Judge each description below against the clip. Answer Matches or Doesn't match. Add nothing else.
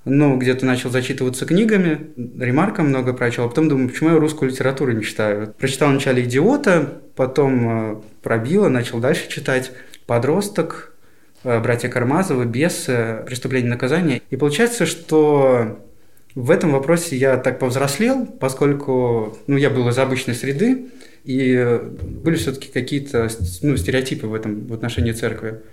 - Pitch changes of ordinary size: Matches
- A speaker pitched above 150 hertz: Doesn't match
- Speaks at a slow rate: Doesn't match